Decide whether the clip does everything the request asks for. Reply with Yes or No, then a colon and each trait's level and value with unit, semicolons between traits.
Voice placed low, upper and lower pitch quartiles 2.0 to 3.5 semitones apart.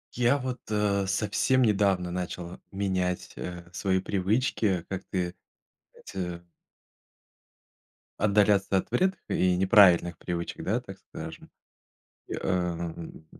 Yes: very low, 95 Hz; average, 2.8 semitones